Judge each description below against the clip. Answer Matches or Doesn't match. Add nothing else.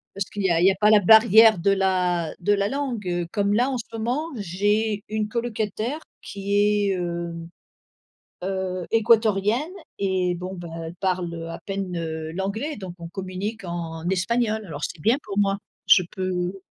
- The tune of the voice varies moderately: Matches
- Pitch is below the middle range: Doesn't match